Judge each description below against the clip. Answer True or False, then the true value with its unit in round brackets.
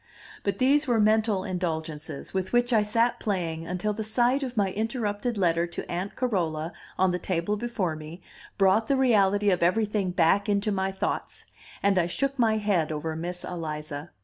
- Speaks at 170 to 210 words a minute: True (175 wpm)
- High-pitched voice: True (195 Hz)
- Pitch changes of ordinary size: True (4.2 semitones)